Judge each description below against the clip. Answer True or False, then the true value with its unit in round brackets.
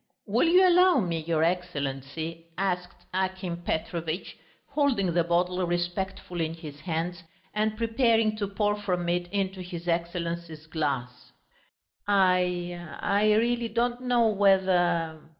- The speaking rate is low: True (125 wpm)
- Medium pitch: True (180 Hz)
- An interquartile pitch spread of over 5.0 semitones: False (3.5 semitones)